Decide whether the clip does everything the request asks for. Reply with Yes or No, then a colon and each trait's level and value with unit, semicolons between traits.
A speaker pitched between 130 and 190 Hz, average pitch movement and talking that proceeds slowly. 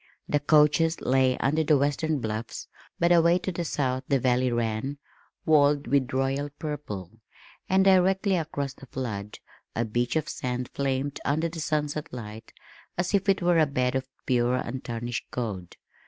No: medium, 140 Hz; average, 4.2 semitones; average, 160 wpm